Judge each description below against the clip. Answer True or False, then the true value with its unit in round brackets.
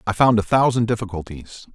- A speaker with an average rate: True (170 wpm)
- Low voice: True (110 Hz)